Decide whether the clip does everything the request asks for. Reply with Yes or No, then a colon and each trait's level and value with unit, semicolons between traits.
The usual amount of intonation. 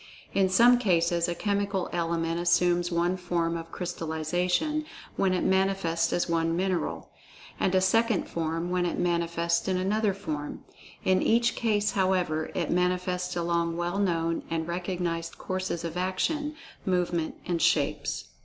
No: narrow, 2.0 semitones